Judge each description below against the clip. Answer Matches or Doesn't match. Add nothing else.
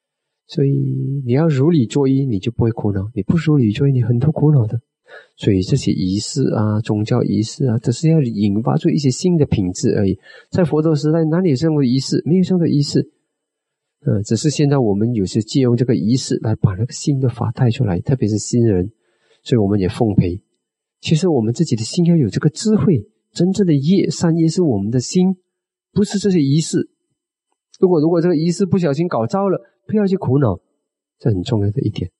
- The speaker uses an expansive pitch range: Matches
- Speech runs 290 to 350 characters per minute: Matches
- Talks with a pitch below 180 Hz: Matches